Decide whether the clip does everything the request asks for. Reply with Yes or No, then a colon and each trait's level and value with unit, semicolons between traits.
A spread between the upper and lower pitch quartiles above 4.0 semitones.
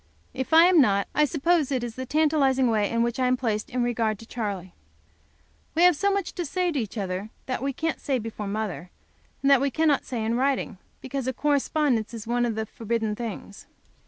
Yes: average, 4.5 semitones